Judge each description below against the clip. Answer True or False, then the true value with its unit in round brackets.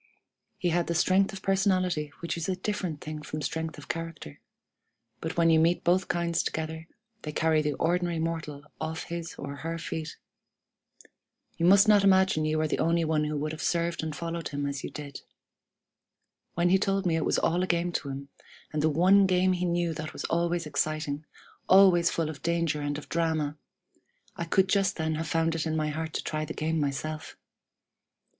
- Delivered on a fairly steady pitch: True (2.2 semitones)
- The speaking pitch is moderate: True (165 Hz)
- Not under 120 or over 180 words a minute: False (200 wpm)